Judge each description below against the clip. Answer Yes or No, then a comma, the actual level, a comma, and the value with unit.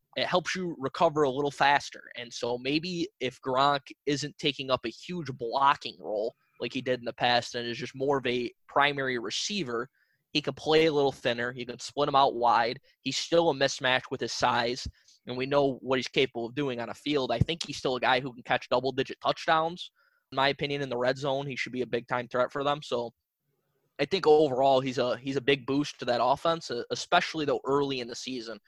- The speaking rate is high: Yes, fast, 230 wpm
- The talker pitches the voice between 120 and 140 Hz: Yes, low, 135 Hz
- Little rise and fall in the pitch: No, average, 3.0 semitones